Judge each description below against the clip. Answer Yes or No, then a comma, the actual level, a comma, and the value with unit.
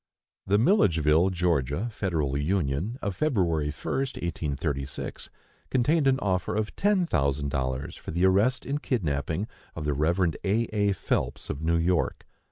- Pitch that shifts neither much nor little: No, wide, 6.4 semitones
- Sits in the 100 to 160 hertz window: No, very low, 90 Hz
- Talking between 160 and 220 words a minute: No, average, 145 wpm